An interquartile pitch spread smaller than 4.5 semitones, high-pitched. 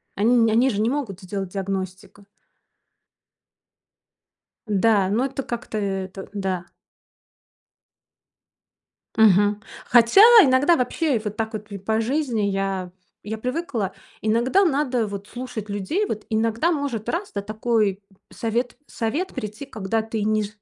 Yes: average, 3.7 semitones; high, 220 Hz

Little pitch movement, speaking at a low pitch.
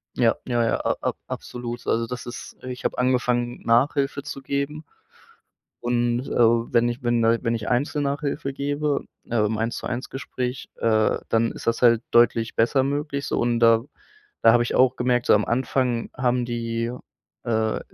Yes: narrow, 2.1 semitones; low, 120 Hz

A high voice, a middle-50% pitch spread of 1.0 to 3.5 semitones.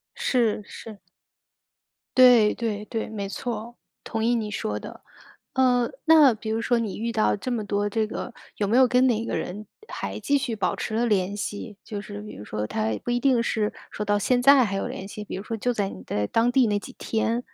Yes: high, 220 Hz; average, 2.8 semitones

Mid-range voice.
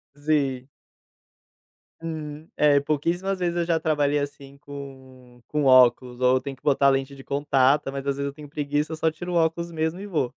Yes: medium, 145 Hz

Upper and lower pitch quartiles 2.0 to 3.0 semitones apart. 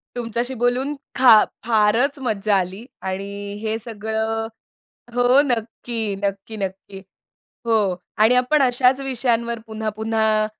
Yes: average, 2.7 semitones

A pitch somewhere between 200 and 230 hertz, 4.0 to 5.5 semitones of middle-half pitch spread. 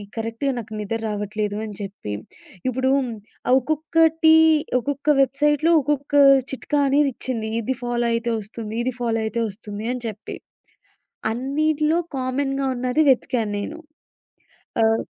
No: very high, 250 Hz; average, 4.4 semitones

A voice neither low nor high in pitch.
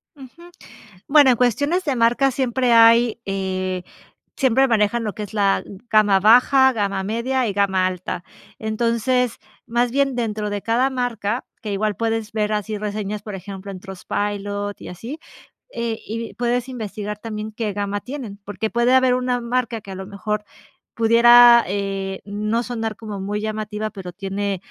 No: high, 215 Hz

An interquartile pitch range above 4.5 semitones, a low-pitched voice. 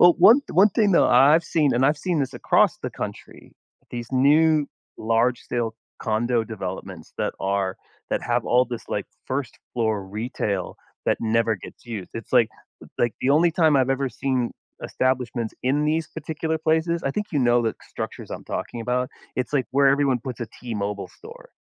Yes: average, 4.9 semitones; low, 130 Hz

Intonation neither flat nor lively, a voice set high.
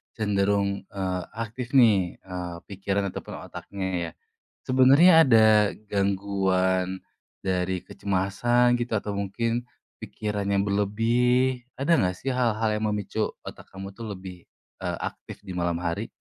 No: average, 3.6 semitones; low, 100 Hz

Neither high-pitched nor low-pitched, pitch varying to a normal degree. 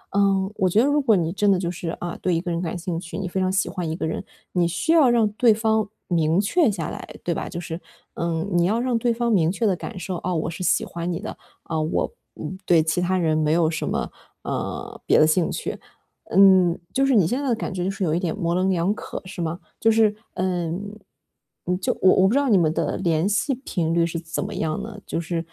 Yes: medium, 180 Hz; average, 3.6 semitones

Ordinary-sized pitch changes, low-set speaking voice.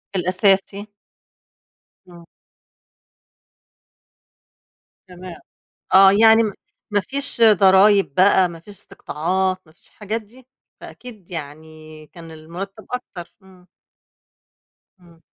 No: average, 3.4 semitones; high, 190 Hz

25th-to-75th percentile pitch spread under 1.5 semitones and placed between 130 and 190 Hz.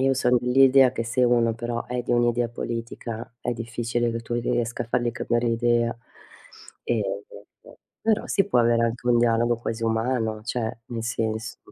No: narrow, 1.0 semitones; low, 120 Hz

